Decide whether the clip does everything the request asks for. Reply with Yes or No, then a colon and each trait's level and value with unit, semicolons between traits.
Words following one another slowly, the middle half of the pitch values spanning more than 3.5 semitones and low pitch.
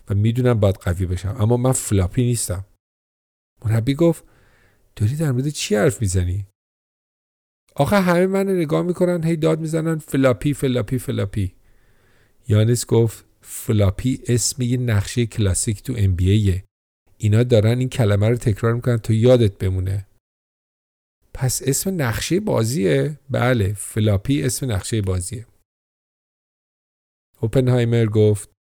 Yes: slow, 125 wpm; average, 4.5 semitones; low, 115 Hz